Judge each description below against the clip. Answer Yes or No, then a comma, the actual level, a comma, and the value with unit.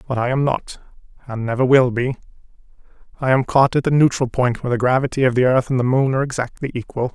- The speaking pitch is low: Yes, low, 125 Hz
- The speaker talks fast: Yes, fast, 225 wpm